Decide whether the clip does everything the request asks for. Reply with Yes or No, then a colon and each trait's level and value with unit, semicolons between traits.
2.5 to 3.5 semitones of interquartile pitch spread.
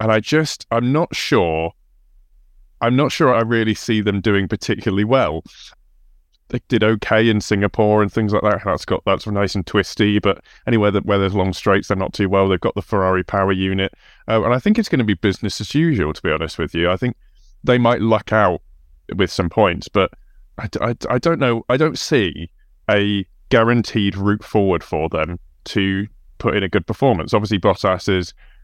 Yes: average, 3.0 semitones